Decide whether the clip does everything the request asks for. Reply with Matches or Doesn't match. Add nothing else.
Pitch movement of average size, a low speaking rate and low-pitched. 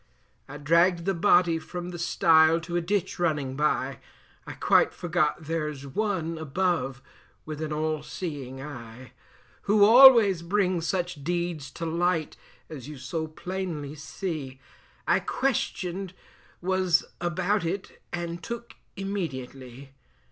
Doesn't match